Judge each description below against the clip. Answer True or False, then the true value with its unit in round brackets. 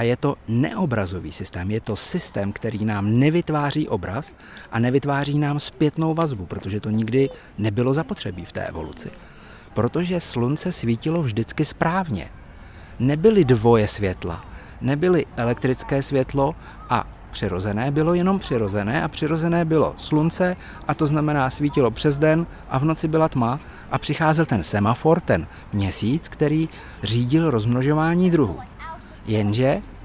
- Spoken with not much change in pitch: False (6.5 semitones)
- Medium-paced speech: True (135 wpm)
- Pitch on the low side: True (130 Hz)